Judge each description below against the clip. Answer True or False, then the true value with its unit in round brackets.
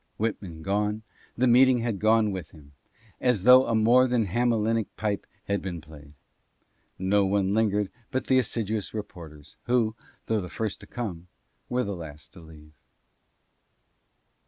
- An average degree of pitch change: True (4.2 semitones)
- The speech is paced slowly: False (160 wpm)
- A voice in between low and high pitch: False (105 Hz)